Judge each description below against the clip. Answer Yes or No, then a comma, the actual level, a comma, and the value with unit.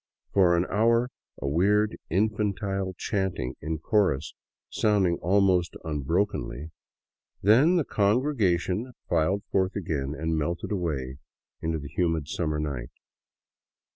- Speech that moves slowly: Yes, slow, 110 wpm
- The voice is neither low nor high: No, very low, 90 Hz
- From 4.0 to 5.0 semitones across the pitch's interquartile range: Yes, average, 4.6 semitones